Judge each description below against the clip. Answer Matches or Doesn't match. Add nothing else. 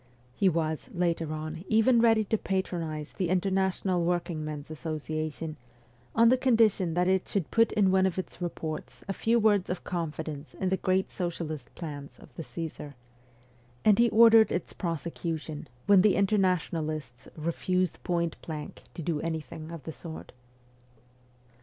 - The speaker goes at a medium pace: Matches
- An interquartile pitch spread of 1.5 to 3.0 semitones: Doesn't match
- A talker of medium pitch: Matches